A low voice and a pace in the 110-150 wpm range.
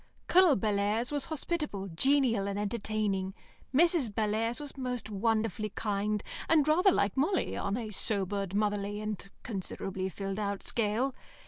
No: high, 215 Hz; slow, 135 wpm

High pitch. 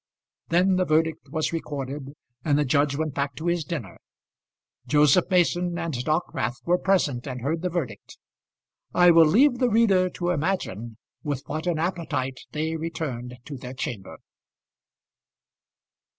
No: medium, 155 Hz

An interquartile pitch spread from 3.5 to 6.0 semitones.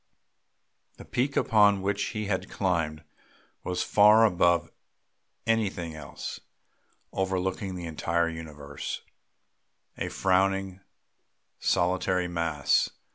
No: average, 3.1 semitones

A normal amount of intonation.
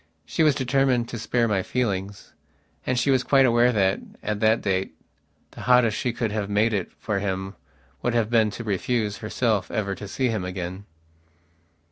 Yes: average, 3.6 semitones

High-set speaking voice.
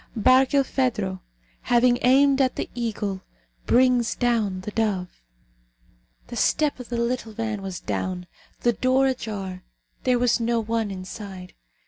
Yes: high, 230 Hz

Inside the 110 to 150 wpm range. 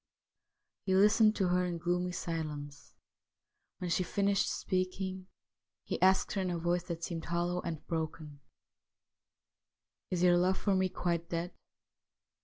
Yes: average, 145 wpm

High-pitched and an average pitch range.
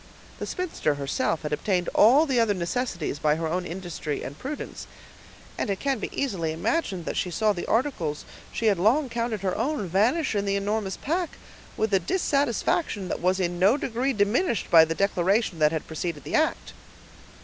No: high, 200 Hz; wide, 6.0 semitones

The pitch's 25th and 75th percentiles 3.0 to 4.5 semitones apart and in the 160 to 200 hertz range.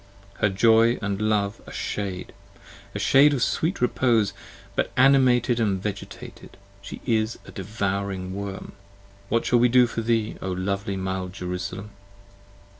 No: average, 3.4 semitones; low, 105 Hz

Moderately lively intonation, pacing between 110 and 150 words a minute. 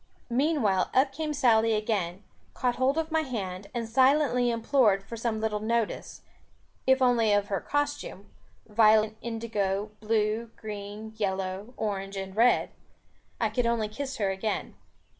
Yes: average, 3.3 semitones; average, 140 wpm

